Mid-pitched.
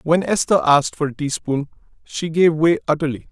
Yes: medium, 155 Hz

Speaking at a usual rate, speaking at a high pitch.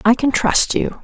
No: fast, 235 wpm; very high, 250 Hz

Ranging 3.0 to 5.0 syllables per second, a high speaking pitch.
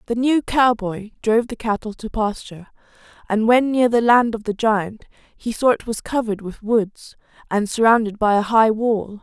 Yes: 4.9 syllables/s; high, 220 Hz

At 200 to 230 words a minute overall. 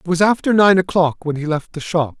No: fast, 275 wpm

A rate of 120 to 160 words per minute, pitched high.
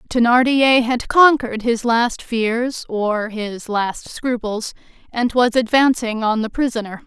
Yes: slow, 135 wpm; high, 235 Hz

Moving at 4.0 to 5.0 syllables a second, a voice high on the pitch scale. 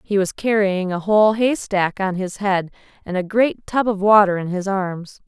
Yes: 4.6 syllables/s; high, 195 Hz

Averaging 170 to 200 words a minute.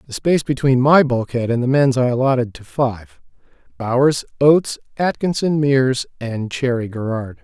No: average, 155 wpm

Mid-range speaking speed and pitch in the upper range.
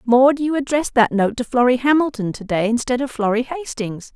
Yes: average, 190 wpm; high, 245 Hz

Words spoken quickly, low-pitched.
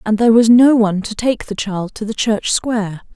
No: fast, 245 wpm; high, 215 Hz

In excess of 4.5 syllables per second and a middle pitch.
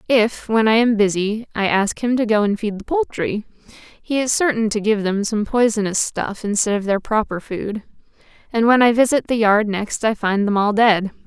No: 4.9 syllables/s; high, 215 Hz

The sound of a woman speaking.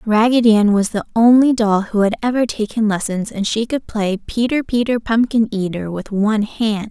Yes: female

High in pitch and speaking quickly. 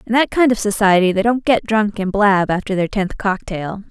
Yes: high, 205 Hz; fast, 230 wpm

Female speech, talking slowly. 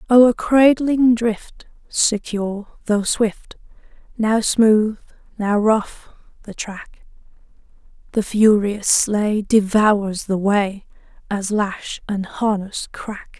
Yes: female; slow, 105 wpm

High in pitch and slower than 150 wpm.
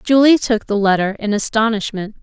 No: high, 220 Hz; average, 160 wpm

